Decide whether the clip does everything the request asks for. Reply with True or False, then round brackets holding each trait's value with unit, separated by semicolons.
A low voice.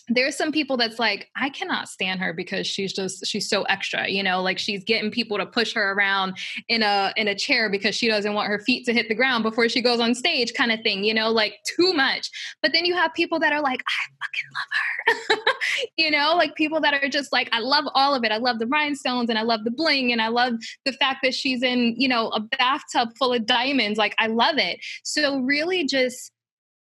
False (240 Hz)